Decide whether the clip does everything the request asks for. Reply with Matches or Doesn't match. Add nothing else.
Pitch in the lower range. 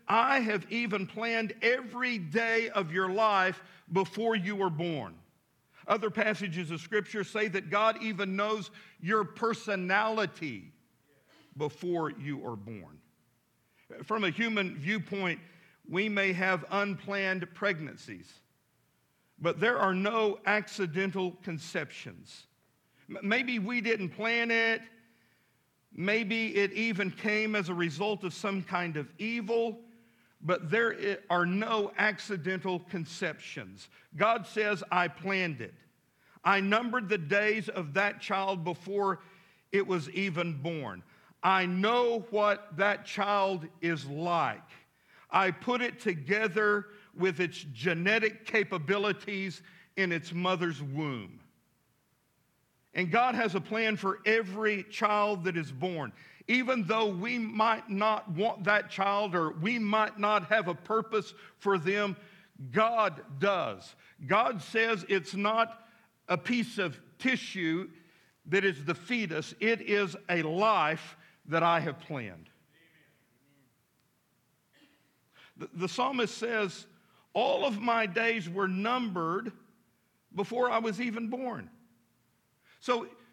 Doesn't match